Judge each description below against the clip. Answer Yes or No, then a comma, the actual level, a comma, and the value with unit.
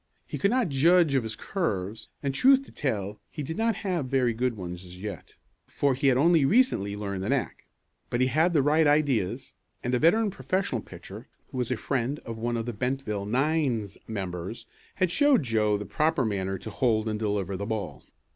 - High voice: No, low, 125 Hz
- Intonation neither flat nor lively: No, wide, 6.7 semitones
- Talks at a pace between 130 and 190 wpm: No, fast, 205 wpm